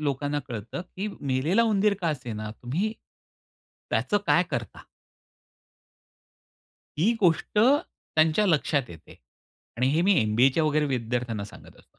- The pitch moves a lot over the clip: Yes, wide, 7.2 semitones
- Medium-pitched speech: Yes, medium, 150 Hz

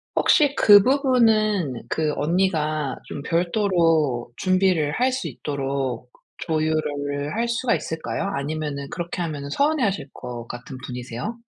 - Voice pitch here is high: No, medium, 155 Hz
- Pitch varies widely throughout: Yes, wide, 6.3 semitones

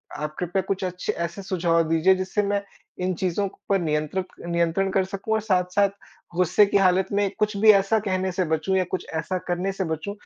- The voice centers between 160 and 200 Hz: Yes, medium, 185 Hz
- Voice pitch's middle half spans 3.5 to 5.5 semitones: No, narrow, 2.5 semitones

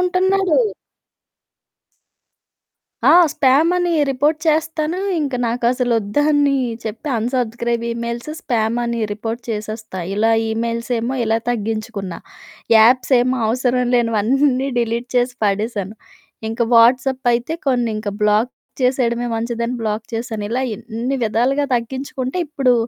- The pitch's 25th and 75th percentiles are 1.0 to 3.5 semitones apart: Yes, average, 2.7 semitones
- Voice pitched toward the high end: Yes, high, 240 Hz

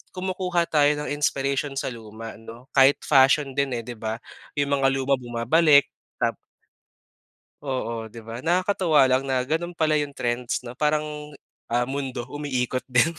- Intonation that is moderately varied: Yes, average, 3.5 semitones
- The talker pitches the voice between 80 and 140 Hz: Yes, low, 135 Hz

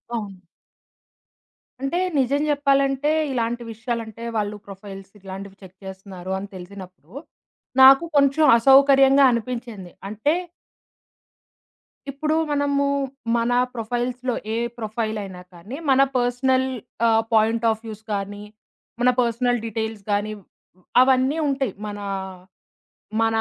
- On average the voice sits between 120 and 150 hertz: No, high, 230 Hz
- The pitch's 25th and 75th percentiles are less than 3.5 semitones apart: No, average, 4.6 semitones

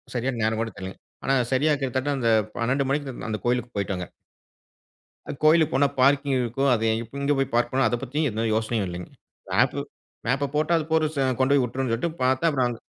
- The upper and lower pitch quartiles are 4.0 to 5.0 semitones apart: No, average, 3.3 semitones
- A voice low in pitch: Yes, low, 130 Hz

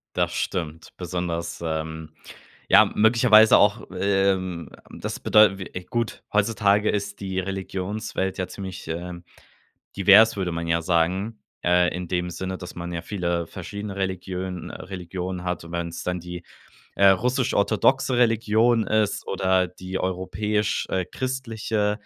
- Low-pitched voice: Yes, very low, 95 Hz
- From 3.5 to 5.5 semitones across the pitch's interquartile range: No, average, 2.9 semitones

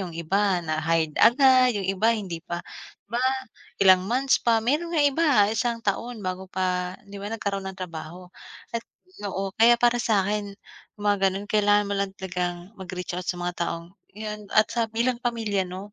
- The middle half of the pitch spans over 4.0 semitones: No, average, 3.7 semitones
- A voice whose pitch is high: Yes, high, 200 Hz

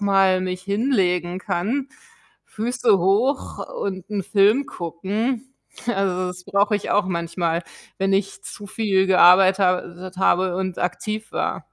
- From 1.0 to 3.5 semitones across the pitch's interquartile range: Yes, narrow, 2.5 semitones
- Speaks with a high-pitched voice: Yes, high, 195 Hz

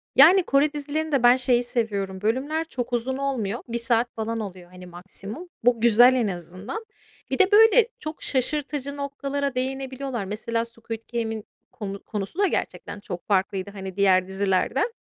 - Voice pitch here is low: No, high, 235 Hz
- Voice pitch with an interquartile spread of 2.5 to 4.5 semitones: No, wide, 5.5 semitones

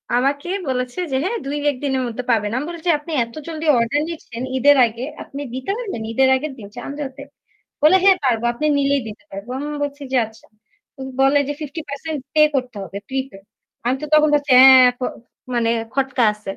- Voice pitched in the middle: No, very high, 270 Hz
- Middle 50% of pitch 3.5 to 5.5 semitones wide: No, average, 3.1 semitones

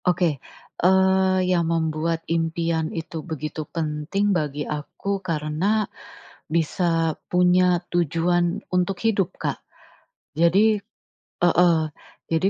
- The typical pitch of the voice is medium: Yes, medium, 170 Hz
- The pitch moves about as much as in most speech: No, narrow, 2.3 semitones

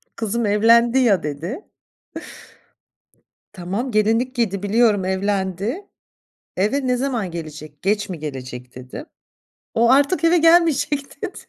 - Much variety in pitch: Yes, wide, 5.7 semitones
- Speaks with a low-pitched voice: No, high, 215 Hz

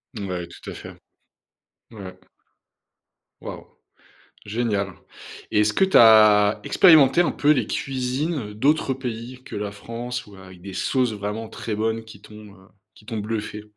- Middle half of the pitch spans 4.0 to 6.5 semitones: No, average, 3.4 semitones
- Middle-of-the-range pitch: No, low, 110 Hz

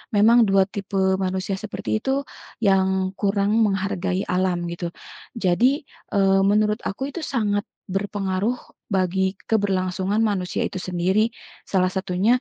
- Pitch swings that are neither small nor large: No, narrow, 1.6 semitones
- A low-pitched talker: No, high, 195 Hz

